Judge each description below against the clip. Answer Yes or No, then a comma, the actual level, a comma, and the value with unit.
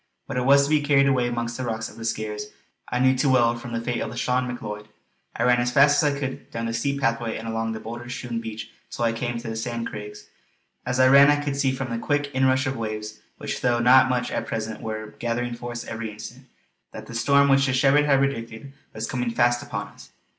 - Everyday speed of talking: No, fast, 245 wpm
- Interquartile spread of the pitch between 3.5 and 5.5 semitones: No, narrow, 2.6 semitones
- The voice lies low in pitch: Yes, low, 120 Hz